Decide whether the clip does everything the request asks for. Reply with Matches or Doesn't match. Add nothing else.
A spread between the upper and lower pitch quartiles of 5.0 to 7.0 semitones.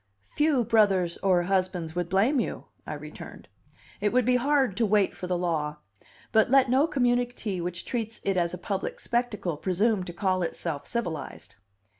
Matches